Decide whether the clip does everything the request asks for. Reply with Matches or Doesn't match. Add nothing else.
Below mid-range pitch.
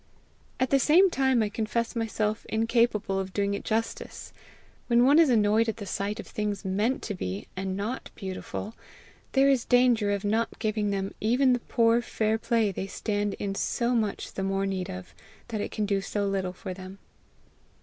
Doesn't match